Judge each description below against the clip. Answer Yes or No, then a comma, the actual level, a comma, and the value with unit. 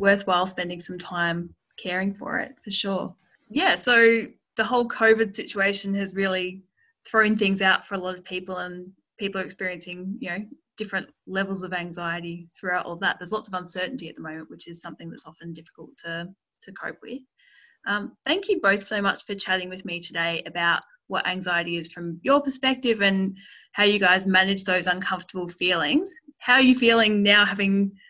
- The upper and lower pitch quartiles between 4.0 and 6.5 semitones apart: No, average, 3.4 semitones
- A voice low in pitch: No, high, 195 Hz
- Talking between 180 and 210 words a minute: Yes, average, 185 wpm